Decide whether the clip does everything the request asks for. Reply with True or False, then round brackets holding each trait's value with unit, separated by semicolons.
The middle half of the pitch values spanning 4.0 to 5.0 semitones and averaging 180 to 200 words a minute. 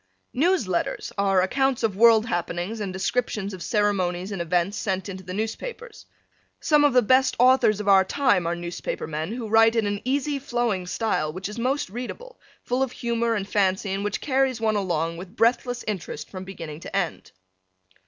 True (4.7 semitones; 185 wpm)